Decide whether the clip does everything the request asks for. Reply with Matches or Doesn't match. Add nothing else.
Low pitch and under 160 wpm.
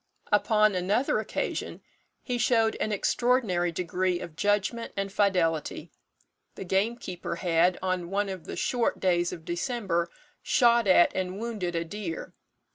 Doesn't match